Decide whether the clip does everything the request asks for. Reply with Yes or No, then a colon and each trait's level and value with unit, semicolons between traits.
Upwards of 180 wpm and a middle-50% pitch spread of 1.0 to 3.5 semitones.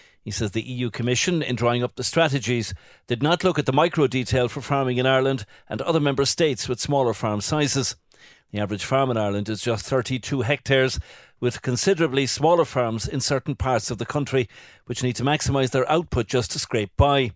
Yes: average, 200 wpm; average, 2.9 semitones